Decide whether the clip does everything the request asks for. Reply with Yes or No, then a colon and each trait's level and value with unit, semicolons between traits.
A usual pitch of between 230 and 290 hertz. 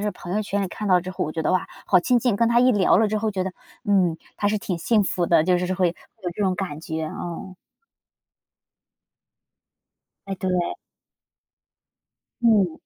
No: high, 190 Hz